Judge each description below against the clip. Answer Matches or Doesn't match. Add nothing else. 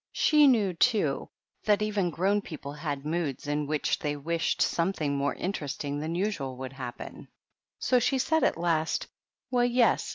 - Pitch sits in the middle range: Matches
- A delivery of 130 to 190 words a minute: Matches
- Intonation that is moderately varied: Doesn't match